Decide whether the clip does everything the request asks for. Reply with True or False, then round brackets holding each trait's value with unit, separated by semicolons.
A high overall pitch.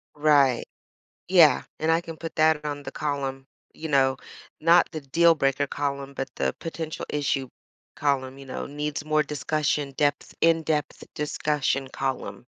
False (145 Hz)